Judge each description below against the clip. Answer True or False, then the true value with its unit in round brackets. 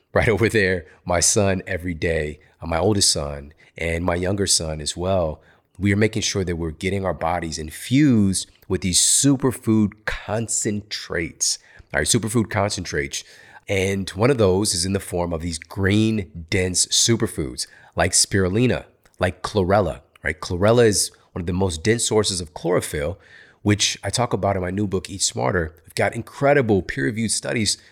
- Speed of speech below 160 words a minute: False (165 wpm)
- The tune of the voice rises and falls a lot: False (3.7 semitones)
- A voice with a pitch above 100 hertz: False (95 Hz)